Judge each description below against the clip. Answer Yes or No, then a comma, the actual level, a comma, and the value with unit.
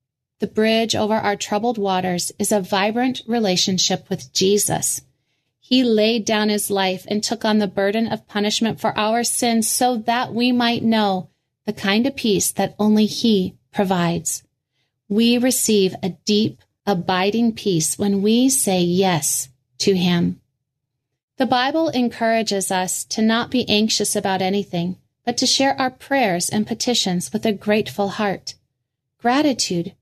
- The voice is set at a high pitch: Yes, high, 205 Hz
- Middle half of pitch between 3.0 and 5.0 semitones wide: Yes, average, 3.8 semitones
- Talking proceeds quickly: No, average, 150 wpm